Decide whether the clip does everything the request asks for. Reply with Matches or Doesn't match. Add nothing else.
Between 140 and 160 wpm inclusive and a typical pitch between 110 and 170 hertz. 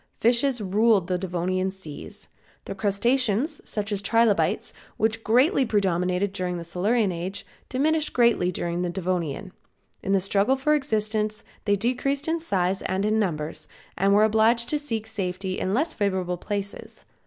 Doesn't match